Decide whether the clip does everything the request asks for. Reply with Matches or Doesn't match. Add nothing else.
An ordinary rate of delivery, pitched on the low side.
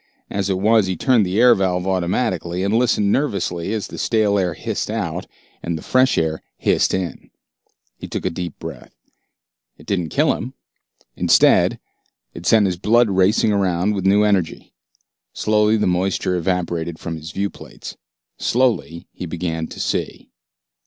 Matches